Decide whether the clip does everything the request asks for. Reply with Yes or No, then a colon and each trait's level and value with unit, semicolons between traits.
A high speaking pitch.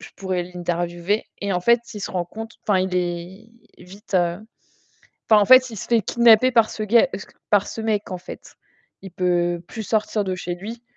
Yes: high, 195 Hz